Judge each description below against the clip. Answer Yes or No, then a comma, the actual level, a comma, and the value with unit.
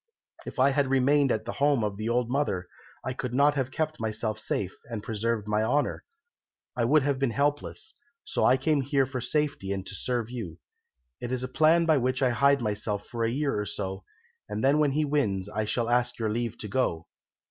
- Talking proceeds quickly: Yes, fast, 215 wpm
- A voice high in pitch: No, low, 125 Hz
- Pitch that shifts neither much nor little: Yes, average, 4.5 semitones